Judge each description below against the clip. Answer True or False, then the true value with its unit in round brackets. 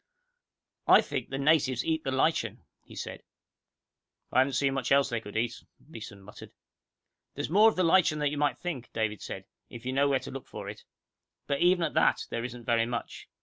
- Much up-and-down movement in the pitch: False (4.5 semitones)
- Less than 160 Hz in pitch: True (135 Hz)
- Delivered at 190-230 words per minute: True (205 wpm)